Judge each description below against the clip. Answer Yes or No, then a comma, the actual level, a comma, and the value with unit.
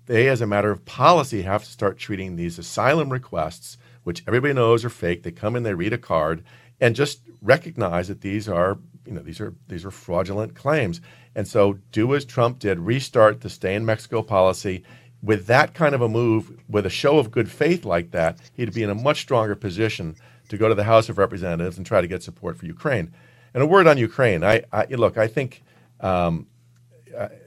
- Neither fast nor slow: No, fast, 215 wpm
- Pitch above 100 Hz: Yes, low, 110 Hz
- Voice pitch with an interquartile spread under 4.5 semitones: Yes, average, 3.7 semitones